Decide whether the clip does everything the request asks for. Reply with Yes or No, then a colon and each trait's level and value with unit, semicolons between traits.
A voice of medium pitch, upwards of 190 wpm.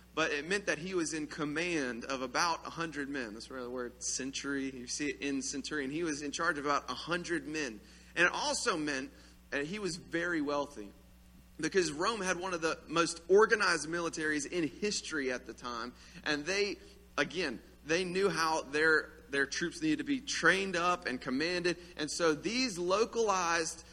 No: medium, 160 Hz; average, 185 wpm